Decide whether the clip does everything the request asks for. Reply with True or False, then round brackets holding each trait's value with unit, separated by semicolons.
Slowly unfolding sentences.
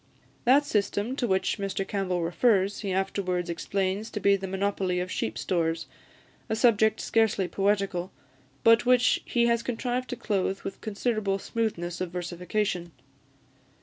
False (145 wpm)